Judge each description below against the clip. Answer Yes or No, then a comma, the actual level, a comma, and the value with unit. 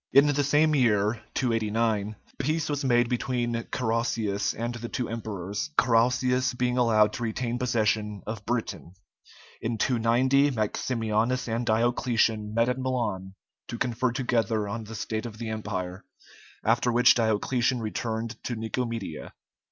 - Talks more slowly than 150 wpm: Yes, slow, 135 wpm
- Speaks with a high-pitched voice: No, low, 115 Hz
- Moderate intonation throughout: No, narrow, 2.3 semitones